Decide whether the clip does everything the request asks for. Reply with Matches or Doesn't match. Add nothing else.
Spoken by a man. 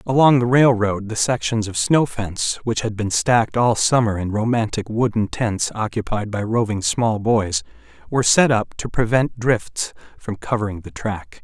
Matches